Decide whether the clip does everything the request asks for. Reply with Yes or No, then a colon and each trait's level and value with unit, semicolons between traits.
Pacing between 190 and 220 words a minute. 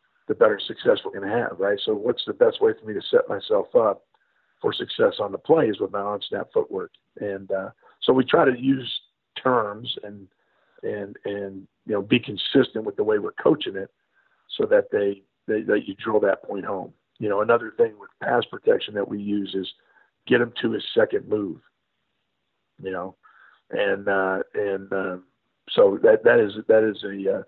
Yes: average, 200 wpm